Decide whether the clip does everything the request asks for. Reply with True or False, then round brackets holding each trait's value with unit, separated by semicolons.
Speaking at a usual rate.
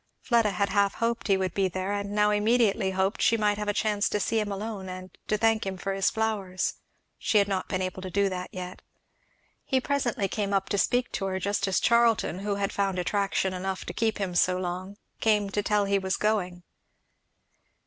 False (215 wpm)